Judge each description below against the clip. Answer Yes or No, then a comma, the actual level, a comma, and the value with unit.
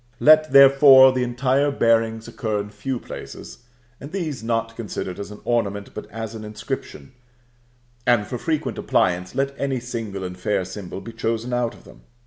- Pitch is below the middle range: Yes, low, 115 Hz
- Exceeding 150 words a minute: Yes, average, 170 wpm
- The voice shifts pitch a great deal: No, average, 4.1 semitones